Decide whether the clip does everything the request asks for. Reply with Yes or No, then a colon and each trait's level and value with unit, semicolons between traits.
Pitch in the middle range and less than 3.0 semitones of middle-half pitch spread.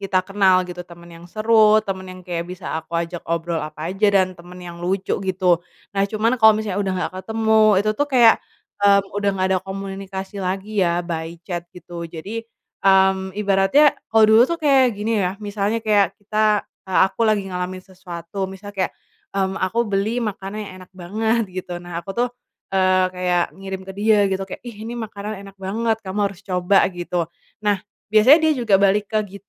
No: high, 195 Hz; narrow, 2.6 semitones